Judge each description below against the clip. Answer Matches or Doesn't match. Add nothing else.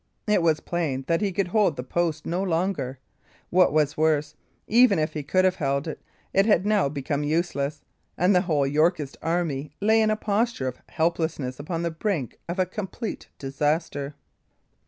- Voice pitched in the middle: Matches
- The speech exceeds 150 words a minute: Matches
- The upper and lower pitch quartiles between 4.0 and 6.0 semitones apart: Matches